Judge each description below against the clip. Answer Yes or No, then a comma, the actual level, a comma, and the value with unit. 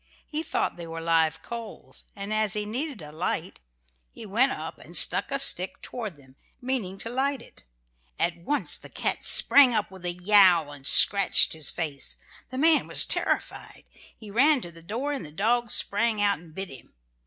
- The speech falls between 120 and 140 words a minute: No, average, 190 wpm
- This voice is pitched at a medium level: No, high, 205 Hz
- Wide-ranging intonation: Yes, wide, 6.5 semitones